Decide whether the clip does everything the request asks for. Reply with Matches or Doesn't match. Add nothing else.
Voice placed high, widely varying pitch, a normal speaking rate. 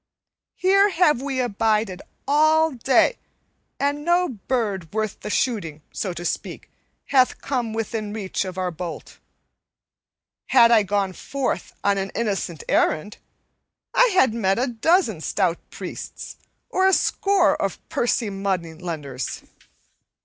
Doesn't match